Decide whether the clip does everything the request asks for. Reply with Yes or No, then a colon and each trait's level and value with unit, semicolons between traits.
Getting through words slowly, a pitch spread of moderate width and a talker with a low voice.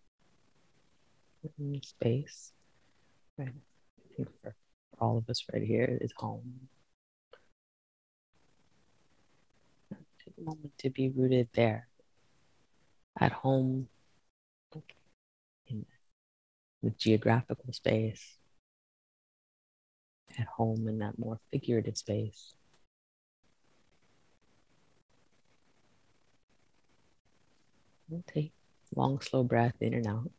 Yes: slow, 85 wpm; average, 3.8 semitones; low, 115 Hz